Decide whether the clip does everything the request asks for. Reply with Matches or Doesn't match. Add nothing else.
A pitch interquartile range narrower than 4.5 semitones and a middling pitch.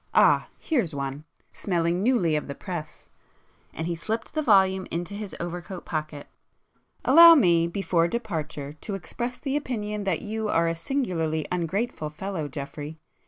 Doesn't match